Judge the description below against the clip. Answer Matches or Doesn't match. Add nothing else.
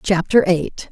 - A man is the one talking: Doesn't match